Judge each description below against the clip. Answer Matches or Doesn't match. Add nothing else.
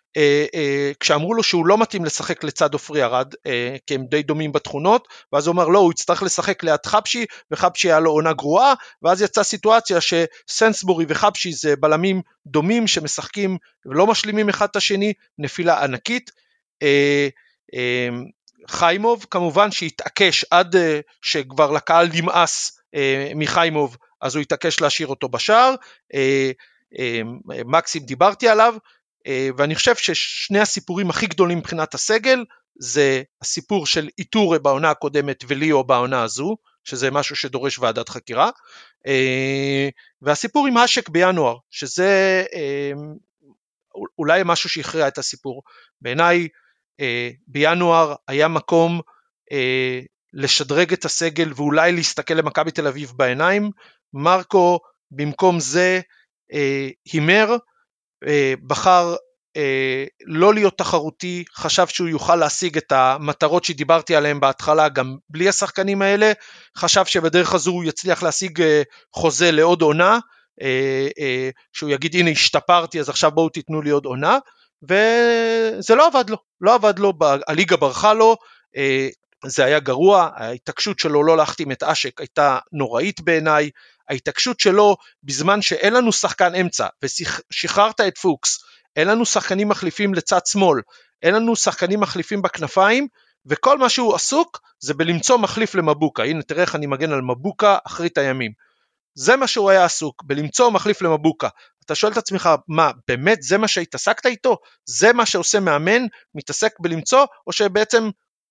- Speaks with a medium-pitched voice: Matches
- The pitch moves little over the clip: Doesn't match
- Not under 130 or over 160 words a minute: Matches